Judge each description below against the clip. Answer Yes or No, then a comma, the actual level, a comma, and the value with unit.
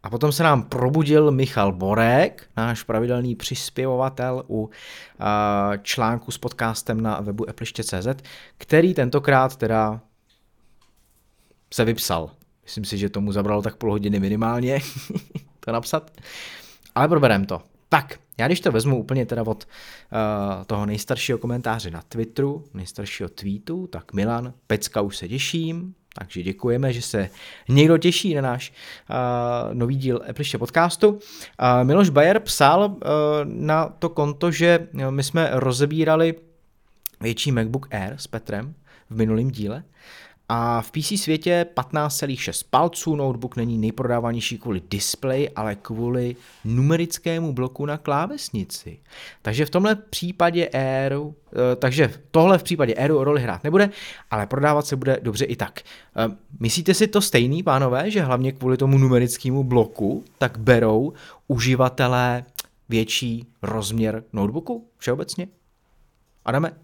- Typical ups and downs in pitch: Yes, average, 5.0 semitones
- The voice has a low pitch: Yes, low, 125 Hz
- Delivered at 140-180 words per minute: No, average, 130 wpm